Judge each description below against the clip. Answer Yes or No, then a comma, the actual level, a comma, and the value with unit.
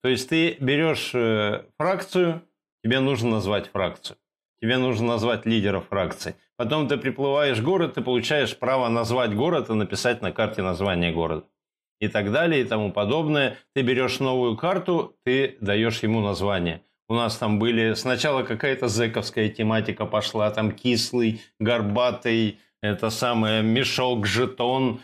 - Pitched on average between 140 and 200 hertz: No, low, 115 Hz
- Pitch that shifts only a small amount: No, average, 3.3 semitones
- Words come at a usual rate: Yes, average, 145 wpm